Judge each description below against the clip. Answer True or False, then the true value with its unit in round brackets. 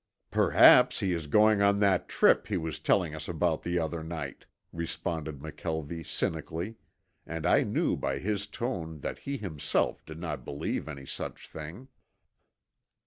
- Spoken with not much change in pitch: False (3.8 semitones)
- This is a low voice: True (80 Hz)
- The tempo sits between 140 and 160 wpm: True (150 wpm)